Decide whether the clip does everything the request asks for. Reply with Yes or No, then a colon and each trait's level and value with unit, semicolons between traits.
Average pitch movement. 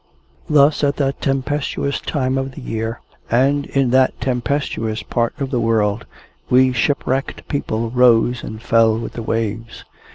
Yes: average, 3.2 semitones